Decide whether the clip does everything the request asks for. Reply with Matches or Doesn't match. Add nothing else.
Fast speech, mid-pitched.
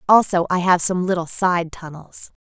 Doesn't match